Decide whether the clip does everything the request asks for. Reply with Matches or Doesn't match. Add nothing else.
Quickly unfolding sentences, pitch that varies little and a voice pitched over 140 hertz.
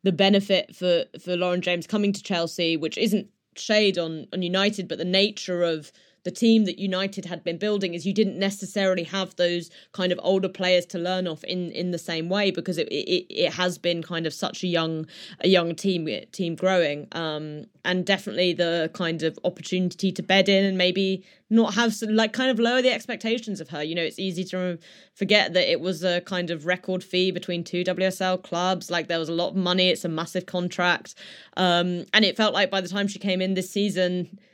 Matches